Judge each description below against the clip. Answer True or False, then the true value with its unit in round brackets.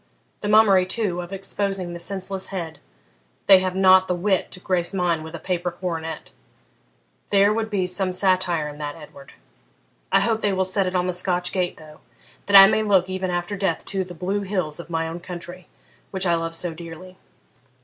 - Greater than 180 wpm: True (200 wpm)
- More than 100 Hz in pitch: True (185 Hz)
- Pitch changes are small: True (2.1 semitones)